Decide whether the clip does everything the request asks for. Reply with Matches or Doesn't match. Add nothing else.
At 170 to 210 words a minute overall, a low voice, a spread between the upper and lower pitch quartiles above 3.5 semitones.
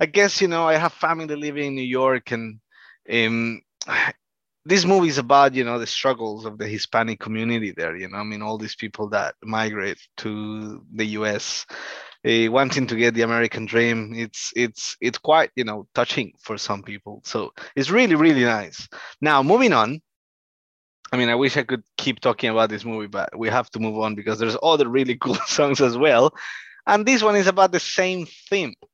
Matches